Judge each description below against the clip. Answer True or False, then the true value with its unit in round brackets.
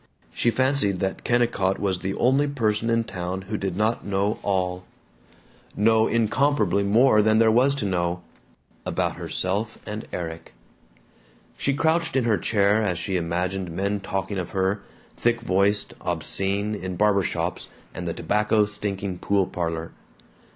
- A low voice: True (100 Hz)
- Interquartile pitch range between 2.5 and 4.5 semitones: True (3.2 semitones)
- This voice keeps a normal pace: True (150 wpm)